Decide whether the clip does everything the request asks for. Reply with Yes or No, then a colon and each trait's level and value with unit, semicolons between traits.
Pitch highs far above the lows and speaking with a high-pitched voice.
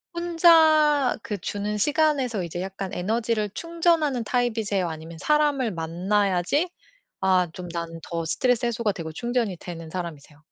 Yes: wide, 7.9 semitones; high, 210 Hz